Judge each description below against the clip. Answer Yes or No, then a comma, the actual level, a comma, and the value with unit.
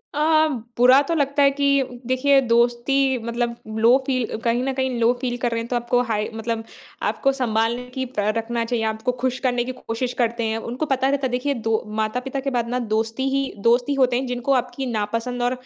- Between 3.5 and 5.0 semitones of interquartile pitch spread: No, narrow, 2.4 semitones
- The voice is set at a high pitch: Yes, high, 245 Hz